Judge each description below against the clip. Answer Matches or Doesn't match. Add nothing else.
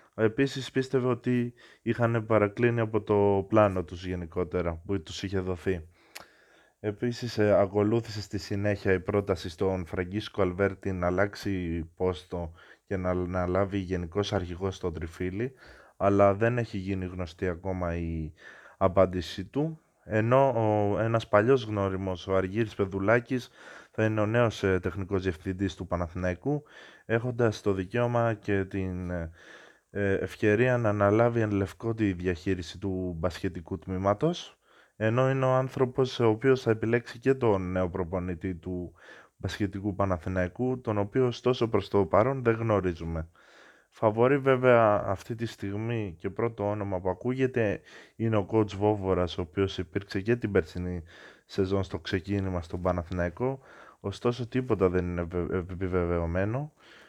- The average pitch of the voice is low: Matches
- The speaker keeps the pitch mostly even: Doesn't match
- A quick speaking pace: Doesn't match